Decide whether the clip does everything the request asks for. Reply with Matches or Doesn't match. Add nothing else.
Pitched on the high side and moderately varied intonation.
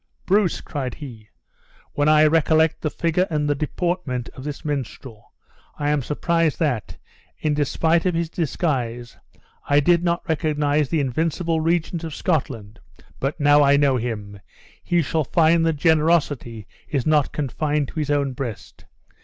Doesn't match